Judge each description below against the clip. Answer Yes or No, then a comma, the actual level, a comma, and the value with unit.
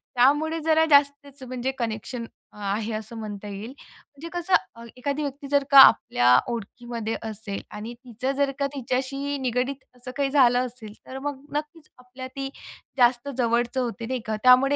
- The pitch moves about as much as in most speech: Yes, average, 3.3 semitones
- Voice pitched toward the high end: Yes, very high, 255 Hz